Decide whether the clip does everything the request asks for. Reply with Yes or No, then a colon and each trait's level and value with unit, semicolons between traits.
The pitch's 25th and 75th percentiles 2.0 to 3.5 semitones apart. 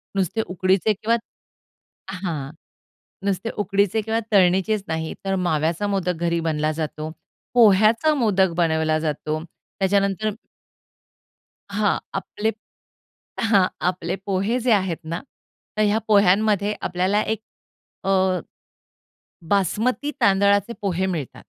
Yes: average, 3.0 semitones